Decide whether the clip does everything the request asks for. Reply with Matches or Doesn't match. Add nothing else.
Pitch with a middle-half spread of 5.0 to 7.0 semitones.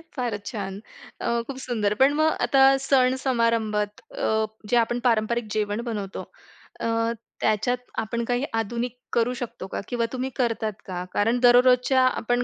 Doesn't match